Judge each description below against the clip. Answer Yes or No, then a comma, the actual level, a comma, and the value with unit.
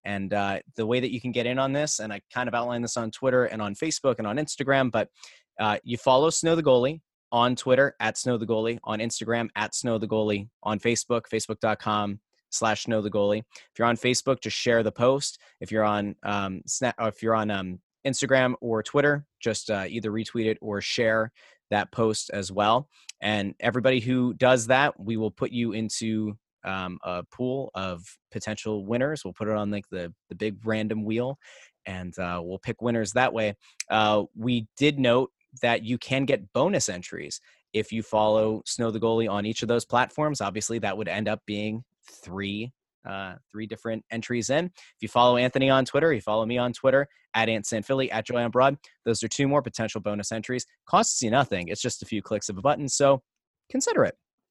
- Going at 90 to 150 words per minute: No, fast, 205 wpm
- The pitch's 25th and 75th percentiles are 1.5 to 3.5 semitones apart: Yes, average, 2.9 semitones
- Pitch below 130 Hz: Yes, low, 115 Hz